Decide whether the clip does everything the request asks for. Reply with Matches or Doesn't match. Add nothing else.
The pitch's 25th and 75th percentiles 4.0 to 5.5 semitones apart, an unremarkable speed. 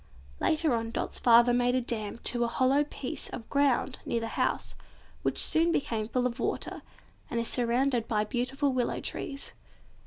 Doesn't match